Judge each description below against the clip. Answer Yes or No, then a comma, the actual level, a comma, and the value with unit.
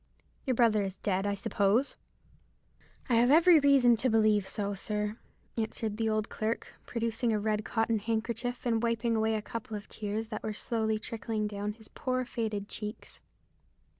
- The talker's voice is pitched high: Yes, high, 220 Hz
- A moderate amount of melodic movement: No, narrow, 1.8 semitones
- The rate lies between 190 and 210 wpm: No, average, 165 wpm